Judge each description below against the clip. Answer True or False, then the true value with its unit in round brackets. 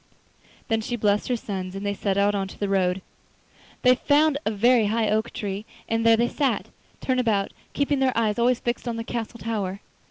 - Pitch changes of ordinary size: True (3.1 semitones)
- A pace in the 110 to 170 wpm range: False (200 wpm)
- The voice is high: True (225 Hz)